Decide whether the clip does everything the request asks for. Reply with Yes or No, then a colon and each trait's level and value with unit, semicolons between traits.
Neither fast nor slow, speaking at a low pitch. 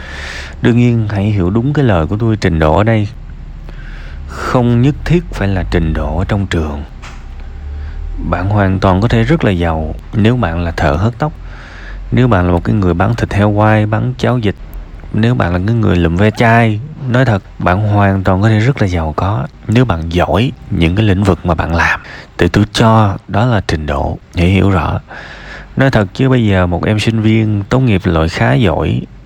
Yes: average, 210 wpm; low, 100 Hz